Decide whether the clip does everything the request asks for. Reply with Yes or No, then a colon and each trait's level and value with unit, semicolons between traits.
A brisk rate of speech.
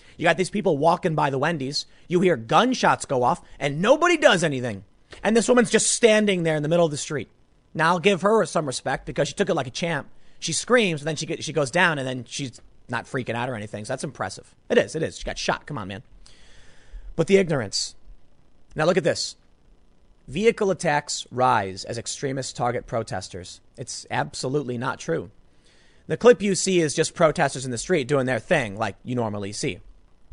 Yes: fast, 210 wpm